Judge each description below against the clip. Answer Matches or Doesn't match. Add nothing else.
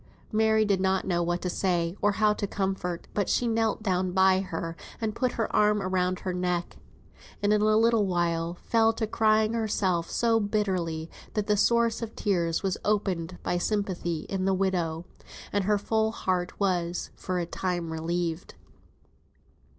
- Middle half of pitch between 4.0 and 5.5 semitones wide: Doesn't match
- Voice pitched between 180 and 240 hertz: Matches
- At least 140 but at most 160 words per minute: Doesn't match